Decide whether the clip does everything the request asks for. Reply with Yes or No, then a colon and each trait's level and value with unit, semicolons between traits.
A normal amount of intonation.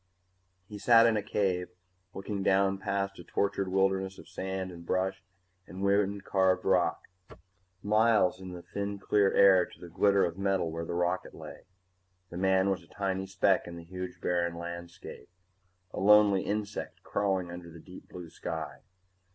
No: narrow, 1.8 semitones